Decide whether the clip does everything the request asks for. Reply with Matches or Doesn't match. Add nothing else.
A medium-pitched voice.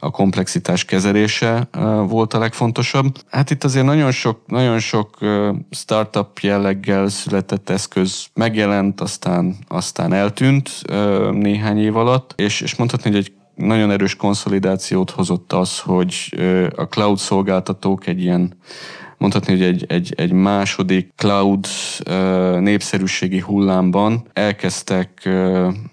Doesn't match